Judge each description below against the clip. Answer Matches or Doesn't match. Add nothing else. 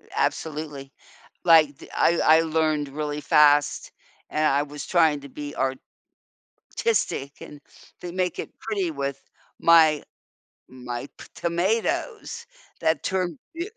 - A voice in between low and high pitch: Matches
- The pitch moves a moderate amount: Matches